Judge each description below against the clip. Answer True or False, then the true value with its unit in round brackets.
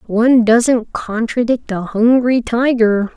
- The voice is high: True (230 Hz)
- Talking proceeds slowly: True (115 wpm)